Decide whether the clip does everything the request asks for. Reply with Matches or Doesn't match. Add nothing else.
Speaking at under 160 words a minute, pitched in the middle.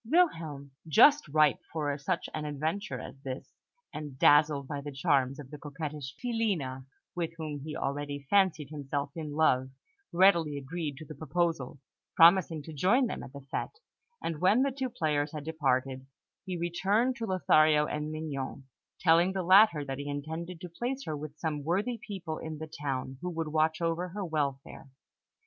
Doesn't match